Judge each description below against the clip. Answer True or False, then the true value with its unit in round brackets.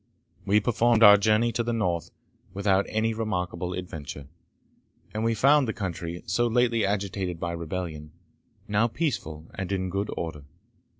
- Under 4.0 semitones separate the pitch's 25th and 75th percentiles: False (4.4 semitones)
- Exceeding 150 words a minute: False (145 wpm)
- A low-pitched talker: True (100 Hz)